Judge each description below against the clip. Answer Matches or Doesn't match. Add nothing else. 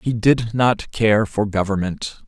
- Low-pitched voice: Matches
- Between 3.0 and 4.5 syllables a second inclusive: Matches